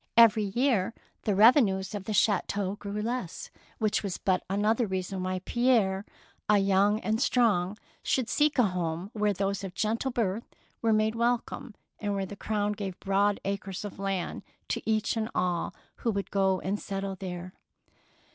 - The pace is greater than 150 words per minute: Yes, average, 170 wpm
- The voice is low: No, high, 205 Hz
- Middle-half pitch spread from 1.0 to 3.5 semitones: Yes, narrow, 2.4 semitones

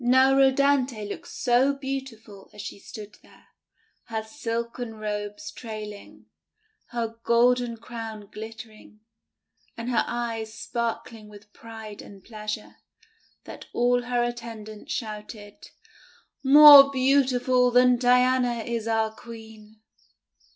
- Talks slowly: Yes, slow, 110 wpm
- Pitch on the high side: Yes, high, 230 Hz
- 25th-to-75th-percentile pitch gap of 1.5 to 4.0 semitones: Yes, narrow, 2.5 semitones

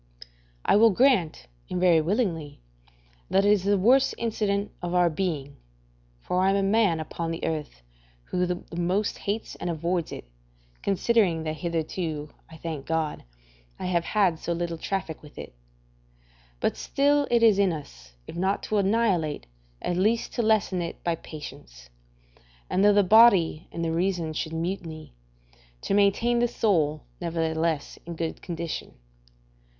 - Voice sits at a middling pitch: Yes, medium, 175 Hz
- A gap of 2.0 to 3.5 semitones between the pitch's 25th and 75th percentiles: No, average, 3.9 semitones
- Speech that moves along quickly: No, average, 155 wpm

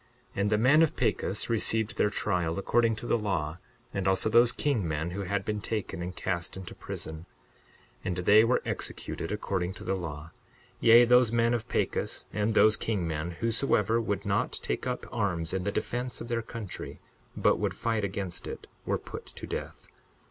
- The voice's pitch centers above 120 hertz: No, low, 105 Hz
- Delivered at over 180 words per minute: Yes, average, 190 wpm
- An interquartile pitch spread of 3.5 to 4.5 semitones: Yes, average, 4.1 semitones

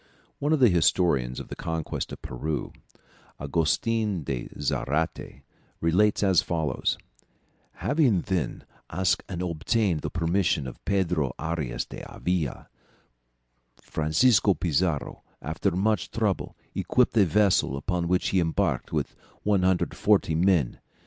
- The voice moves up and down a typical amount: Yes, average, 4.3 semitones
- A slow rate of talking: Yes, slow, 115 wpm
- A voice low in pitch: Yes, very low, 85 Hz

